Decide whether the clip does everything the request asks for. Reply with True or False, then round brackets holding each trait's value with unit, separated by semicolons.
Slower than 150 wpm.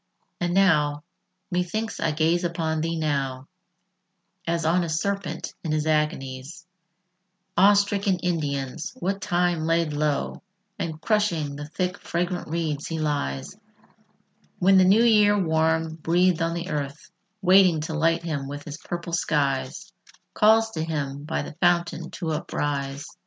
True (140 wpm)